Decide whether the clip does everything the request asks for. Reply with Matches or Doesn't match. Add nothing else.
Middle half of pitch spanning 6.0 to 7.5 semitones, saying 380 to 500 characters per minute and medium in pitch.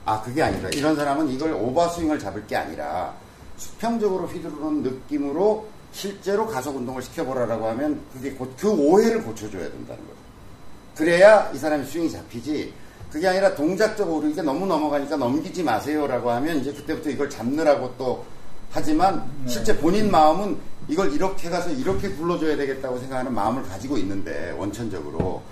Doesn't match